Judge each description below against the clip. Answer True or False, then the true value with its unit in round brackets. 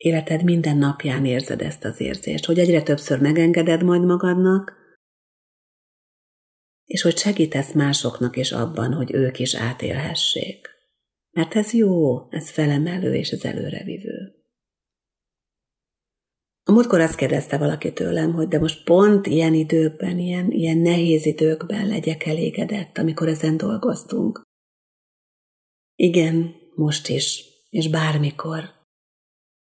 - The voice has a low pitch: False (160 Hz)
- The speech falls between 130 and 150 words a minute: False (115 wpm)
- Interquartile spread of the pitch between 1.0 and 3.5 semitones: True (2.6 semitones)